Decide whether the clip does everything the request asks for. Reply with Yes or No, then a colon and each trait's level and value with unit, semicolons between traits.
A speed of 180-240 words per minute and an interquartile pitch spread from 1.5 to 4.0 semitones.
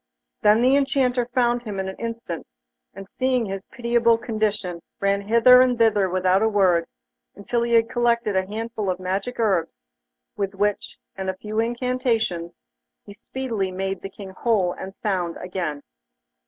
No: average, 160 wpm; average, 3.7 semitones